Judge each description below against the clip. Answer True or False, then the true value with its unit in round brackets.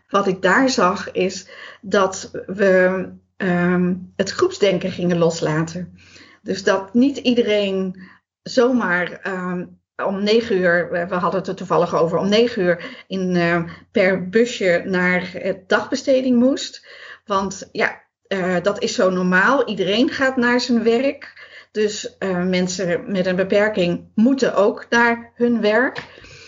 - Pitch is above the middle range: True (195 Hz)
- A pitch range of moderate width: True (4.5 semitones)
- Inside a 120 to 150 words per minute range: True (140 wpm)